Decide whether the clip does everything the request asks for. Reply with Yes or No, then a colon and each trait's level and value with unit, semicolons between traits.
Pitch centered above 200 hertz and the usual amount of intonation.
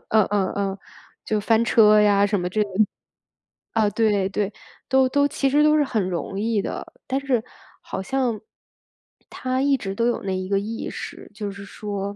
Yes: high, 215 Hz; average, 3.8 semitones